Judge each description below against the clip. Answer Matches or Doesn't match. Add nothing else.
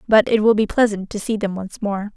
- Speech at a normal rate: Doesn't match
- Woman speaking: Matches